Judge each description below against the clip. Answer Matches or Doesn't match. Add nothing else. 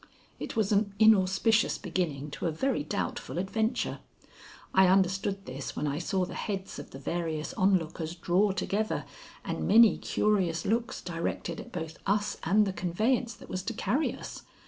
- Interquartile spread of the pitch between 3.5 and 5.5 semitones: Matches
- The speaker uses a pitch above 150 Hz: Matches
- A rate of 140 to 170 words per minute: Matches